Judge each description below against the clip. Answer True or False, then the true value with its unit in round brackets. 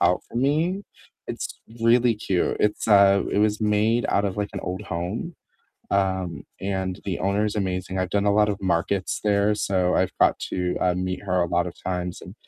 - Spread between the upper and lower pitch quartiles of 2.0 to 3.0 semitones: True (2.4 semitones)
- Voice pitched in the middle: False (100 Hz)